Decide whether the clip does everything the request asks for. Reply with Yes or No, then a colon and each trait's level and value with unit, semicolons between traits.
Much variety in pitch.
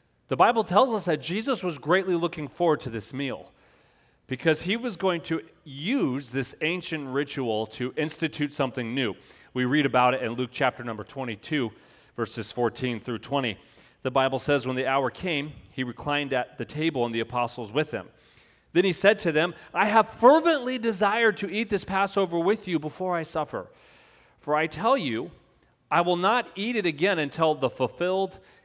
Yes: wide, 6.3 semitones